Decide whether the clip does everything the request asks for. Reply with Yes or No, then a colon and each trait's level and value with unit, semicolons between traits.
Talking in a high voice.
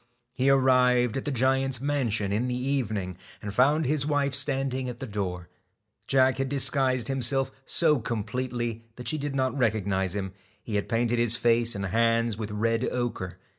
No: low, 125 Hz